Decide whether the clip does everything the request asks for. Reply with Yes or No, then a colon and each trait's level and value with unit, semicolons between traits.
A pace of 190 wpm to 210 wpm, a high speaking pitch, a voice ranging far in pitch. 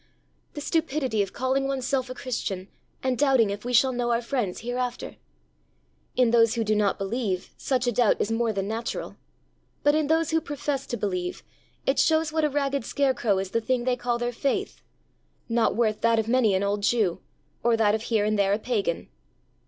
No: average, 200 wpm; high, 240 Hz; average, 3.7 semitones